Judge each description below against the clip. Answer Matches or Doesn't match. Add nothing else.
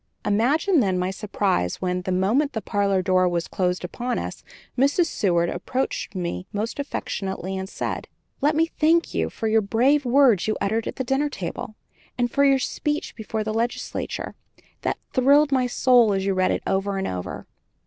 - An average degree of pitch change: Doesn't match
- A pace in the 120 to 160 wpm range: Doesn't match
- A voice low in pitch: Doesn't match